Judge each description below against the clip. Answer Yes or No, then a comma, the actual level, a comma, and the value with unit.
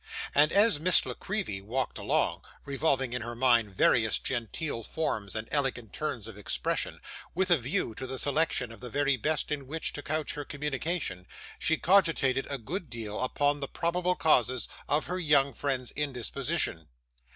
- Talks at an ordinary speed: Yes, average, 170 wpm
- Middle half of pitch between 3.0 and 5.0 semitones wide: Yes, average, 4.7 semitones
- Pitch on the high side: No, medium, 140 Hz